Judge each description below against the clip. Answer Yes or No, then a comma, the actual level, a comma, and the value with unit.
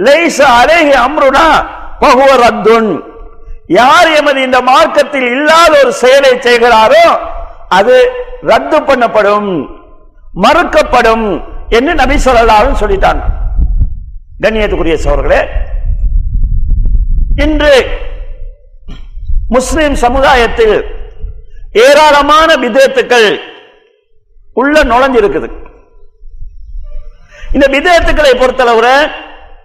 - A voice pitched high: Yes, very high, 270 Hz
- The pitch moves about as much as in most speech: No, wide, 6.4 semitones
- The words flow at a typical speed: No, slow, 40 wpm